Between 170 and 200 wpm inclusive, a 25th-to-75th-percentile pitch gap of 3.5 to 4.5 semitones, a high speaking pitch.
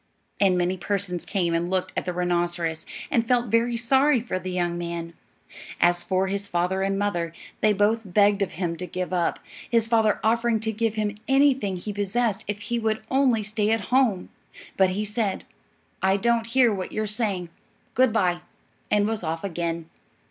Yes: average, 185 wpm; average, 3.9 semitones; high, 200 Hz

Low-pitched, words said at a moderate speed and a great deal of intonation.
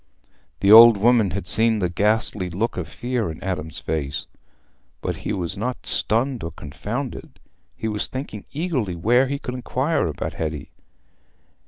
Yes: low, 105 Hz; average, 155 wpm; wide, 5.9 semitones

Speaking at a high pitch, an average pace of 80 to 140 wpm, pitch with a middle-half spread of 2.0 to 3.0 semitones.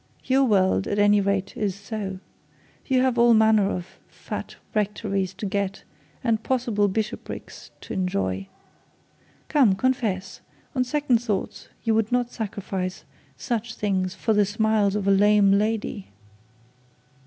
Yes: high, 210 Hz; slow, 135 wpm; average, 2.7 semitones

